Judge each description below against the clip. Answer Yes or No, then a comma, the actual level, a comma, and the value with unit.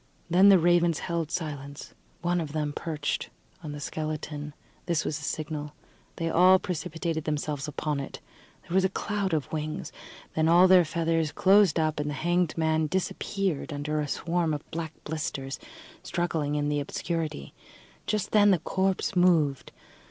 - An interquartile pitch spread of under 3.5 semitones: Yes, average, 2.8 semitones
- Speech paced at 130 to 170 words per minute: Yes, average, 160 wpm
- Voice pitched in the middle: Yes, medium, 160 Hz